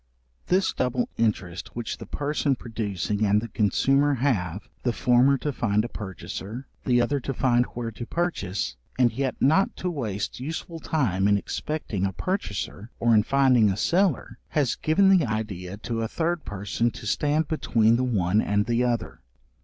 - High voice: No, low, 120 Hz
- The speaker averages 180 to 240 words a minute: No, average, 170 wpm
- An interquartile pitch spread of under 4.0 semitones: No, average, 5.1 semitones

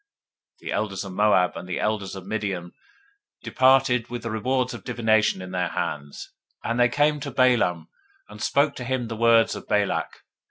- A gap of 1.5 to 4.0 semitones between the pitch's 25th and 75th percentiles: No, average, 4.6 semitones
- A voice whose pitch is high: No, low, 110 Hz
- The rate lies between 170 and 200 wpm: Yes, average, 185 wpm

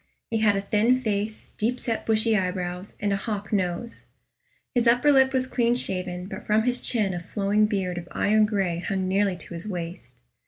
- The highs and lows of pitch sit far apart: No, average, 3.6 semitones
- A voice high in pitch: Yes, high, 205 Hz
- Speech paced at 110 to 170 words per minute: No, average, 195 wpm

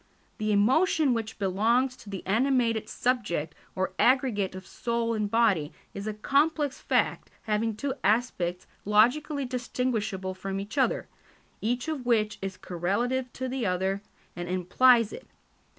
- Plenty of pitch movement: No, average, 4.5 semitones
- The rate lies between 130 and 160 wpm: Yes, average, 140 wpm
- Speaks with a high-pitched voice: Yes, high, 225 Hz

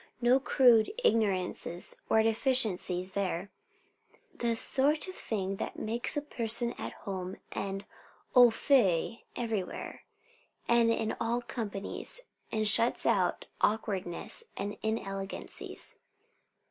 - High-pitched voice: Yes, high, 220 Hz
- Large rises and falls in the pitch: No, average, 3.4 semitones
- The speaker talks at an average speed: No, slow, 110 wpm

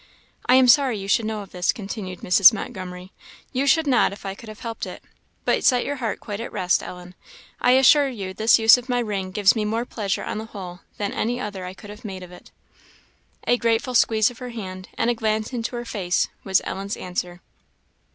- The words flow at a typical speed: No, fast, 220 wpm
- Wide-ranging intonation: No, average, 4.0 semitones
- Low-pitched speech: No, high, 215 Hz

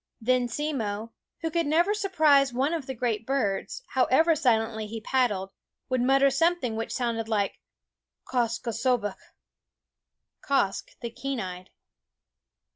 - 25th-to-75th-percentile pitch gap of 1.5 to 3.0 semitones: No, average, 3.8 semitones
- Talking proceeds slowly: Yes, slow, 130 wpm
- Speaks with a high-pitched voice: Yes, very high, 250 Hz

